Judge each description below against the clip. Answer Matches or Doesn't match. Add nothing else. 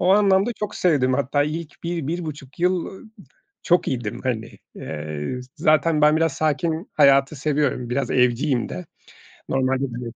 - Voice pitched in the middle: Matches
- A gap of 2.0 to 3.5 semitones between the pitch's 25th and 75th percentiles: Doesn't match